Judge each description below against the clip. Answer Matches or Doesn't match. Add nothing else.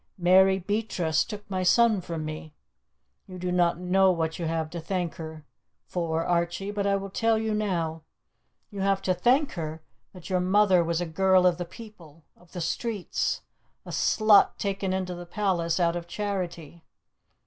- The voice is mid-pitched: Matches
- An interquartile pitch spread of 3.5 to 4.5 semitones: Doesn't match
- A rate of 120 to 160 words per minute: Doesn't match